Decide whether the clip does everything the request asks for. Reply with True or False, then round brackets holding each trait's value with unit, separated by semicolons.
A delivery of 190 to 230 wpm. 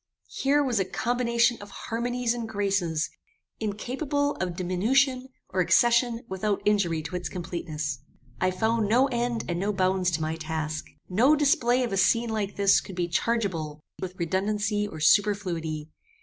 False (155 wpm)